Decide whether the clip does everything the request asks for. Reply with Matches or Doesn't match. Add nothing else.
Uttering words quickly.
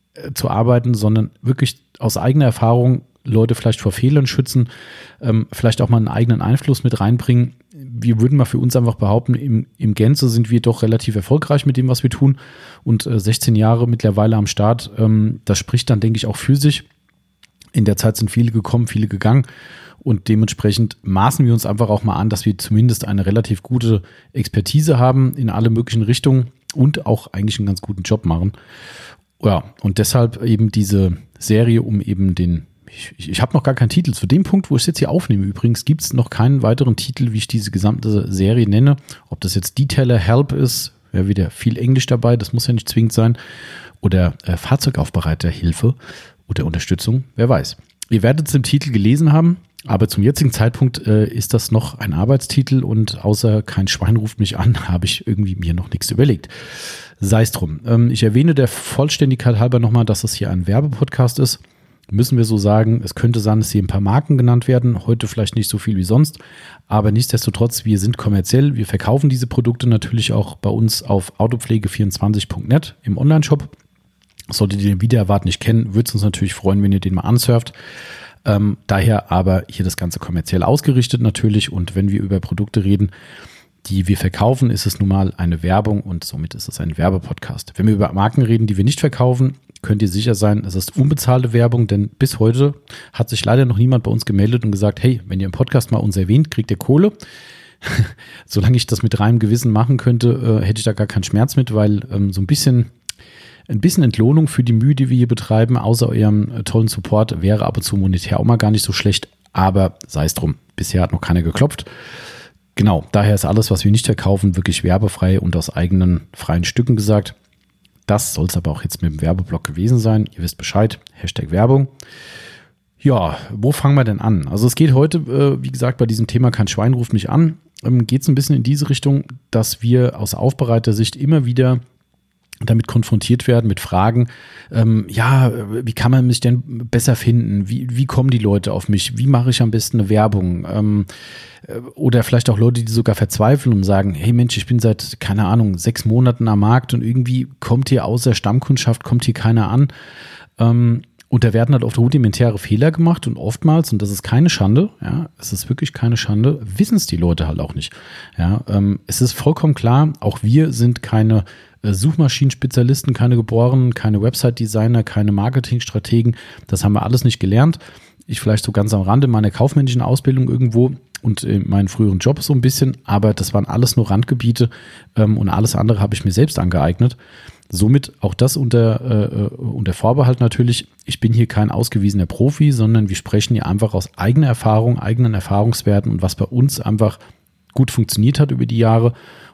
Matches